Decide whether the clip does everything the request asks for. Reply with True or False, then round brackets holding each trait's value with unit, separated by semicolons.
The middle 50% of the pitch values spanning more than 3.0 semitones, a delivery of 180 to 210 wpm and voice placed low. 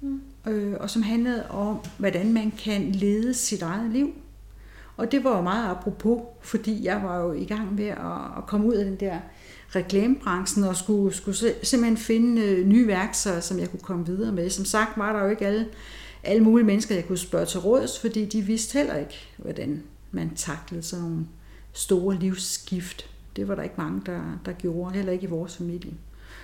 False (3.5 semitones; 190 wpm; 200 Hz)